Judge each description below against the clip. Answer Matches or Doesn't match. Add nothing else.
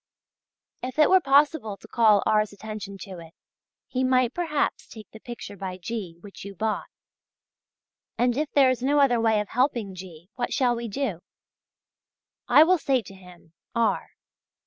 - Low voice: Doesn't match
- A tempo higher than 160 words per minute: Matches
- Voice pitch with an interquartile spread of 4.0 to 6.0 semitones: Matches